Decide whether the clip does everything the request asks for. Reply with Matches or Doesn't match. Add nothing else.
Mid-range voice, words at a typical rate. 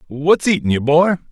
Matches